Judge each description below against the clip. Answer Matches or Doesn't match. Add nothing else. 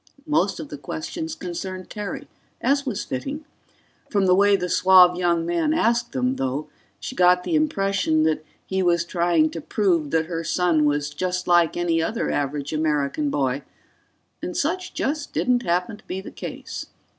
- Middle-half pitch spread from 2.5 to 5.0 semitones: Doesn't match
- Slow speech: Doesn't match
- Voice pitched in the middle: Matches